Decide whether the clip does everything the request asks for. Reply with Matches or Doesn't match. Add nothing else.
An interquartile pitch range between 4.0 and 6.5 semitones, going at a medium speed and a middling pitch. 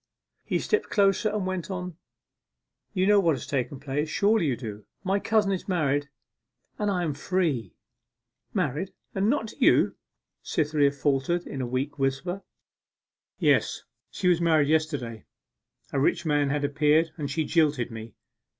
Matches